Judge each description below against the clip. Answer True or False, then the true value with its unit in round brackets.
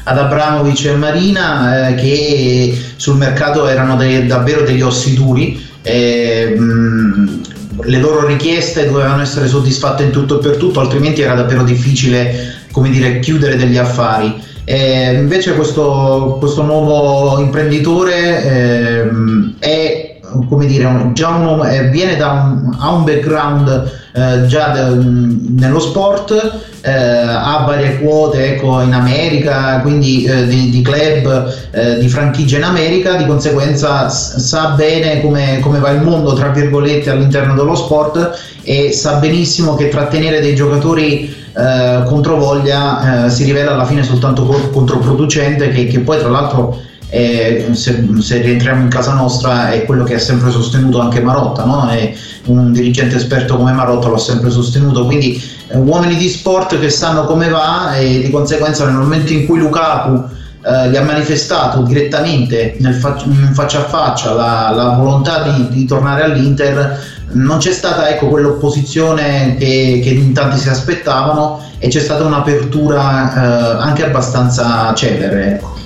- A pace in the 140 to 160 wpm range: True (145 wpm)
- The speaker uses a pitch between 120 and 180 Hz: True (135 Hz)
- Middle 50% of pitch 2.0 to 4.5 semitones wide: True (2.9 semitones)